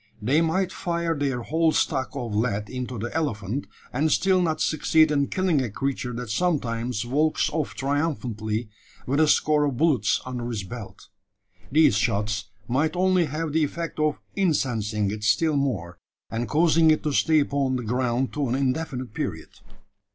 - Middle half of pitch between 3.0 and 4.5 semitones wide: No, average, 5.1 semitones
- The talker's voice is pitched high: No, low, 135 Hz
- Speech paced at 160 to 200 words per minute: Yes, average, 165 wpm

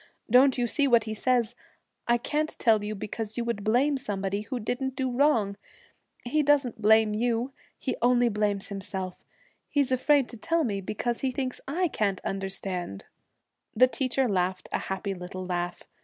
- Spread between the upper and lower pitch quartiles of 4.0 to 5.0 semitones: Yes, average, 4.5 semitones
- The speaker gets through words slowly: No, average, 170 wpm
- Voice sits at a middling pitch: No, high, 230 Hz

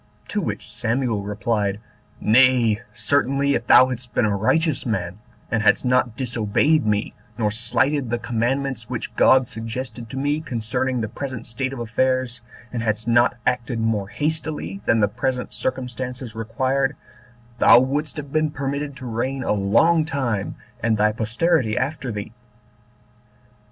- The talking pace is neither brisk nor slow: Yes, average, 150 wpm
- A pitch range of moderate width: Yes, average, 3.4 semitones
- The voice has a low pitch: Yes, low, 125 Hz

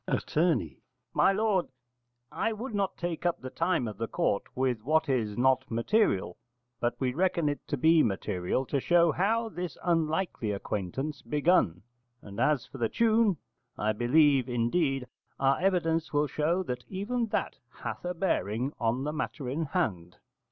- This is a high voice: No, medium, 150 Hz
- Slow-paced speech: No, average, 160 wpm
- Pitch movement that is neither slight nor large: No, wide, 6.7 semitones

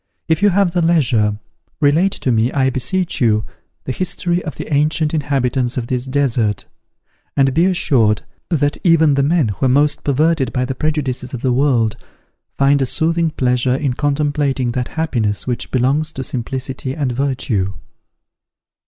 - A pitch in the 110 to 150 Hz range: Yes, low, 135 Hz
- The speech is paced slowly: No, average, 160 wpm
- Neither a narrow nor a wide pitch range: Yes, average, 3.7 semitones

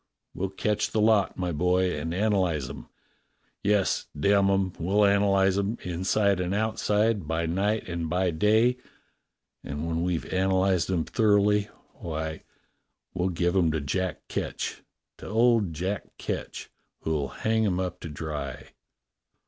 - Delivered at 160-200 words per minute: No, average, 150 wpm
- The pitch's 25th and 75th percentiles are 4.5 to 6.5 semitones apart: No, average, 3.5 semitones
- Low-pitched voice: Yes, very low, 95 Hz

